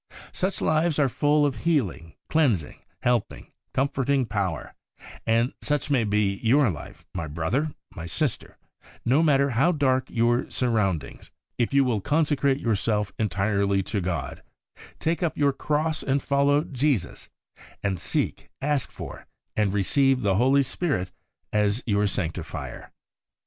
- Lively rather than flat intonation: Yes, wide, 6.0 semitones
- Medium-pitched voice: No, low, 125 Hz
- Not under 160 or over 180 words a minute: No, slow, 135 wpm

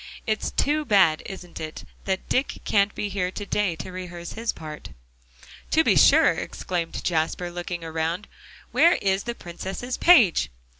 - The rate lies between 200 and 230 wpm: No, average, 155 wpm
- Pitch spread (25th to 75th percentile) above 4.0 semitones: No, average, 3.4 semitones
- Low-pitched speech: No, medium, 185 Hz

